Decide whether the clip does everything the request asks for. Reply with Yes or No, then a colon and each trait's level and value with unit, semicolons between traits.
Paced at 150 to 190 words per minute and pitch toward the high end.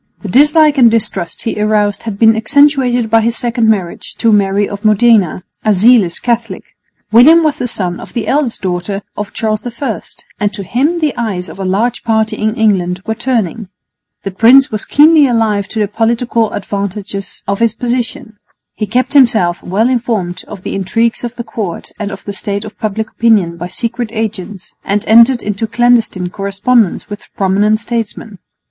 Yes: average, 180 wpm; high, 220 Hz